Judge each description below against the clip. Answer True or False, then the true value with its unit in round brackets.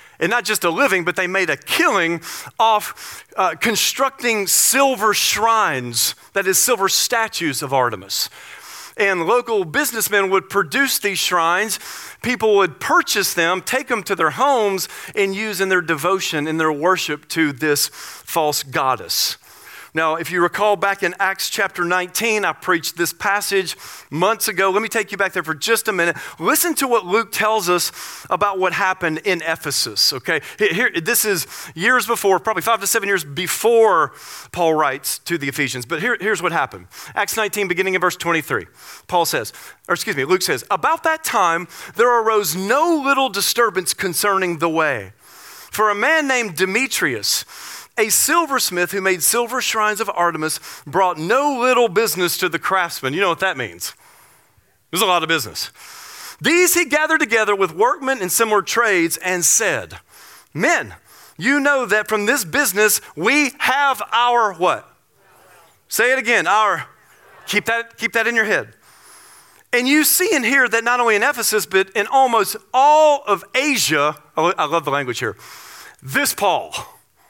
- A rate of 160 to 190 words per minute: True (170 wpm)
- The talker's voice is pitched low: False (200 Hz)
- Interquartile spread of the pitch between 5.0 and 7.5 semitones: True (5.4 semitones)